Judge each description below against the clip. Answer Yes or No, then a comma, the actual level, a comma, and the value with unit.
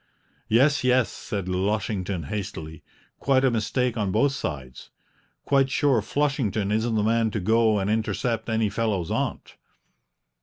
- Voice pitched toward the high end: No, low, 110 Hz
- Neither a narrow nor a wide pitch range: Yes, average, 3.9 semitones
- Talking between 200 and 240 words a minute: No, average, 140 wpm